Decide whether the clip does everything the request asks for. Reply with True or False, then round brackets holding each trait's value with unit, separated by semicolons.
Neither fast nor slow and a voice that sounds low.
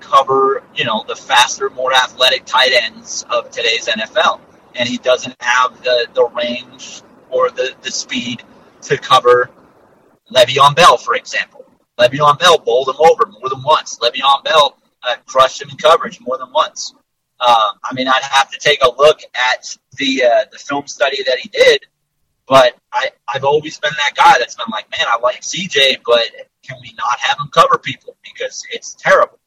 False (185 wpm; 165 Hz)